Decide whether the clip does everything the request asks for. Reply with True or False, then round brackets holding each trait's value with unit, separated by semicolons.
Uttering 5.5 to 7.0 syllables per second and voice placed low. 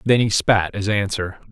False (4.6 syllables/s; 100 Hz)